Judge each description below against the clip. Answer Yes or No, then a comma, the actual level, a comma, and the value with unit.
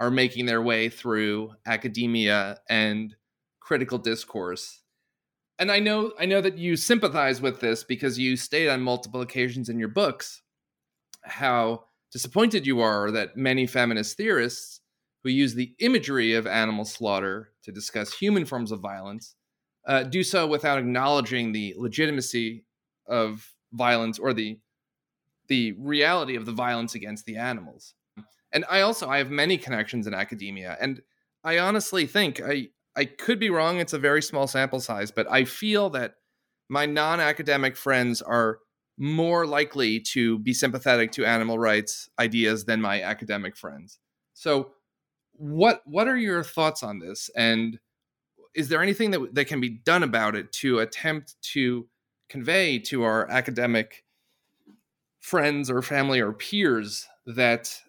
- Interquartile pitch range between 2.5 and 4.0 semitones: No, average, 4.8 semitones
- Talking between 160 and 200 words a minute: No, average, 150 wpm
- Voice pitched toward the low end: Yes, low, 125 Hz